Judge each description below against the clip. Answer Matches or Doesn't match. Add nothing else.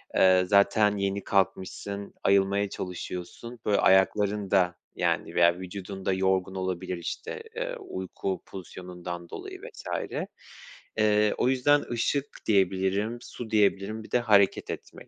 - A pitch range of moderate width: Doesn't match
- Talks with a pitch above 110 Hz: Doesn't match